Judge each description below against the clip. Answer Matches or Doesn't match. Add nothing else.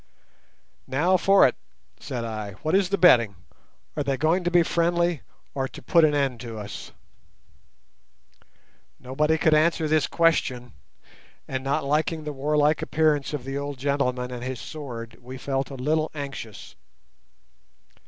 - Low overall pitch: Doesn't match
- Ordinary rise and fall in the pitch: Matches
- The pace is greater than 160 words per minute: Doesn't match